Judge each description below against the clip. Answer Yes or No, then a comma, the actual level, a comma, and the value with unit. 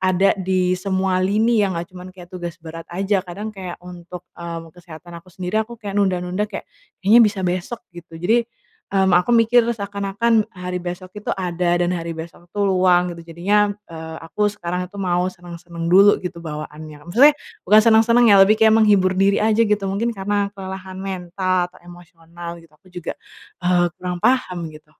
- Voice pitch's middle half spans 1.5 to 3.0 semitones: Yes, average, 2.7 semitones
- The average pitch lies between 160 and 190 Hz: Yes, medium, 185 Hz